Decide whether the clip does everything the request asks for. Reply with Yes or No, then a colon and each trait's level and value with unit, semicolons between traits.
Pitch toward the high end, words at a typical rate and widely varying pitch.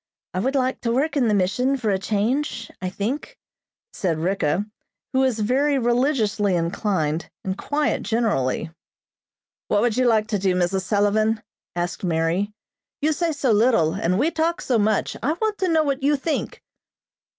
Yes: high, 220 Hz; average, 170 wpm; wide, 6.2 semitones